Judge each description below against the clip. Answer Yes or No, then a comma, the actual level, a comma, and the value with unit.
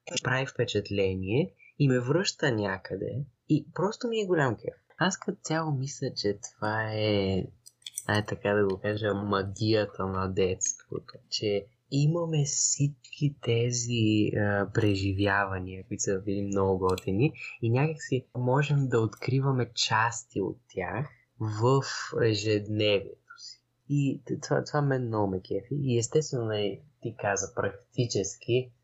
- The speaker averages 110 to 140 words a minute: Yes, average, 130 wpm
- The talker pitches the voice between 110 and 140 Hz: Yes, low, 120 Hz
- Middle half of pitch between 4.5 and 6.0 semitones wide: Yes, average, 5.2 semitones